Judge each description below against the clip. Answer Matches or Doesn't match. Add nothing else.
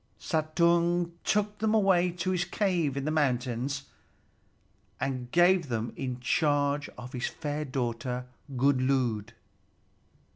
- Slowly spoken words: Matches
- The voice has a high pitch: Doesn't match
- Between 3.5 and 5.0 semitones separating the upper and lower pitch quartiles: Doesn't match